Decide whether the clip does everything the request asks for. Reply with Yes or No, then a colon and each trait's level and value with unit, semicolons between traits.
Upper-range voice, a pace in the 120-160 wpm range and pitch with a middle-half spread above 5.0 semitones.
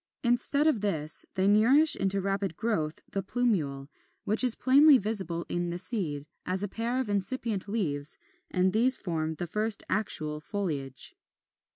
Yes: high, 200 Hz; average, 155 wpm; wide, 5.4 semitones